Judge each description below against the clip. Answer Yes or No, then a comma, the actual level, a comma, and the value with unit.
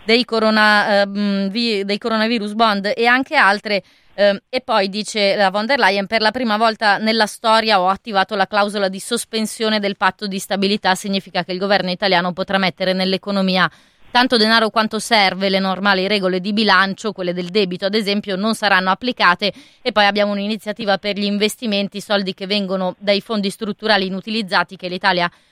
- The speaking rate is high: Yes, fast, 175 wpm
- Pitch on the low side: No, high, 205 Hz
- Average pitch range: No, narrow, 2.2 semitones